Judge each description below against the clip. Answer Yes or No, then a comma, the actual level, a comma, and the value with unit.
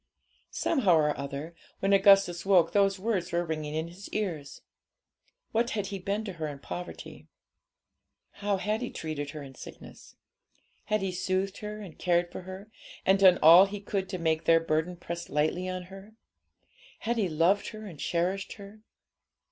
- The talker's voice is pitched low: No, medium, 185 Hz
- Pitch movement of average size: Yes, average, 3.3 semitones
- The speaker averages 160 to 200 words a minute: Yes, average, 170 wpm